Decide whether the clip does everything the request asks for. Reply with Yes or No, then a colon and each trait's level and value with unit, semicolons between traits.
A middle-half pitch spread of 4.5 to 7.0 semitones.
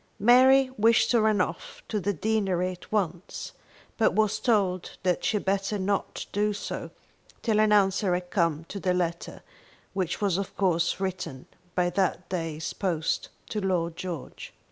No: average, 3.0 semitones